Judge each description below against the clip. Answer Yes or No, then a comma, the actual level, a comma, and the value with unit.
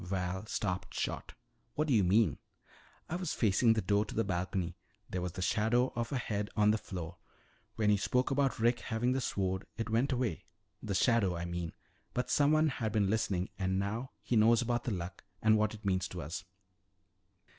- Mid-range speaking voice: No, low, 105 Hz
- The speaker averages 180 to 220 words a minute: Yes, average, 200 wpm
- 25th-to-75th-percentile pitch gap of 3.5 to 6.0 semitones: Yes, average, 4.2 semitones